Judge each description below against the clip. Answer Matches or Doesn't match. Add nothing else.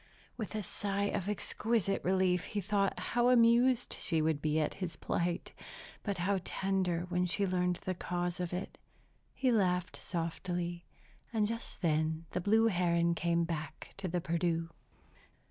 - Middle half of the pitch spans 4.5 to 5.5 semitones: Doesn't match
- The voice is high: Doesn't match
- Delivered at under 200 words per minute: Matches